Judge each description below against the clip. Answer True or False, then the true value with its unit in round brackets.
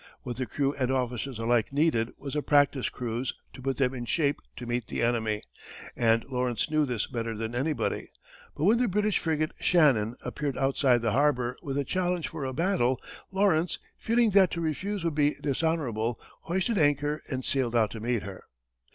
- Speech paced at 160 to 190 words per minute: True (185 wpm)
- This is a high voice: False (135 Hz)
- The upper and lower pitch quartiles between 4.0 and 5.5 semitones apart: True (4.8 semitones)